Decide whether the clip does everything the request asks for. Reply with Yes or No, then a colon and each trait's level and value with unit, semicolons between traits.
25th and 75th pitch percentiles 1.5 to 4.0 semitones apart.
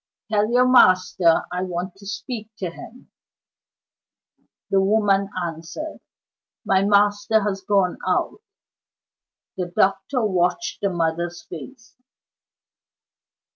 Yes: average, 2.8 semitones